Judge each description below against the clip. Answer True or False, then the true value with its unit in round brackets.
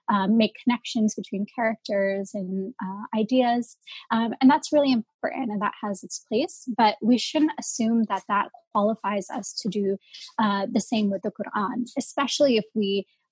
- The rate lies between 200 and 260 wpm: False (165 wpm)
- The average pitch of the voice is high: True (225 Hz)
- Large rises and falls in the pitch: False (3.7 semitones)